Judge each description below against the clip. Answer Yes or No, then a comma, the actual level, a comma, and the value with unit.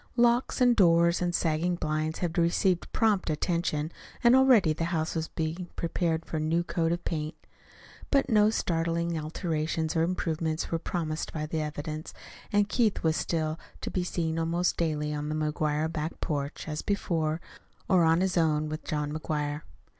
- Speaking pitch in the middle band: Yes, medium, 165 Hz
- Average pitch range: No, narrow, 2.1 semitones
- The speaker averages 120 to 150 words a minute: No, average, 170 wpm